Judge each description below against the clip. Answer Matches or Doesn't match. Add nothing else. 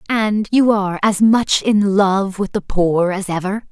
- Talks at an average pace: Matches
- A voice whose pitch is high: Matches